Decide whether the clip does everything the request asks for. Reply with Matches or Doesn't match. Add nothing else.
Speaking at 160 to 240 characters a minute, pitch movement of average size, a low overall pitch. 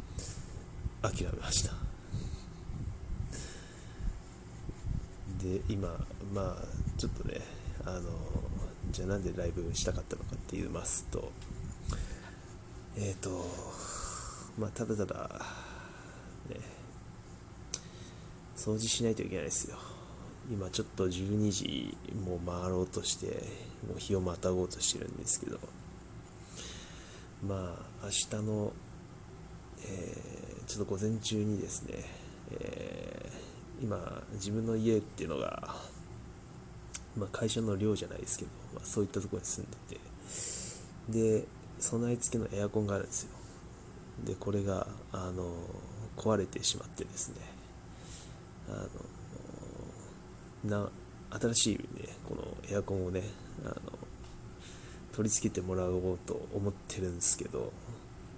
Matches